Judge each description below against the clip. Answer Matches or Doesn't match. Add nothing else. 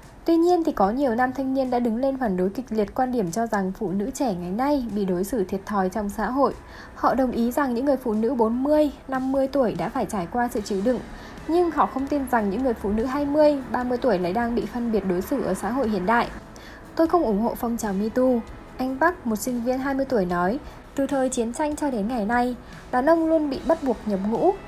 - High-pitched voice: Matches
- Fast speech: Matches